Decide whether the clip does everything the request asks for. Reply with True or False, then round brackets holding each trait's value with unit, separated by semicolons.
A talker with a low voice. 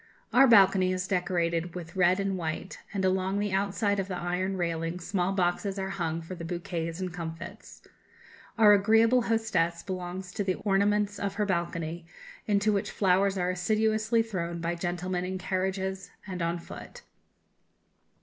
False (185 Hz)